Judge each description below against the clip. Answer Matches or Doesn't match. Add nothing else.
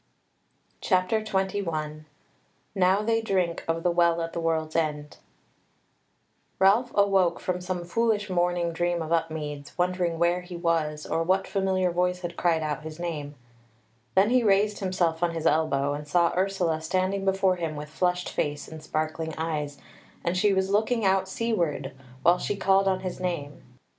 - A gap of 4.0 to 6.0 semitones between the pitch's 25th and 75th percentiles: Doesn't match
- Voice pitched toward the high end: Doesn't match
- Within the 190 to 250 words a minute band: Doesn't match